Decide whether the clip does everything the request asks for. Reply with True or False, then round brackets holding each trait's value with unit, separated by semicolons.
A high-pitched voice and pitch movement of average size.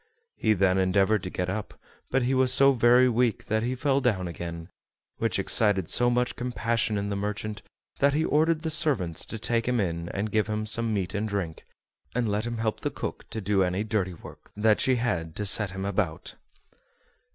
False (110 Hz; 4.1 semitones)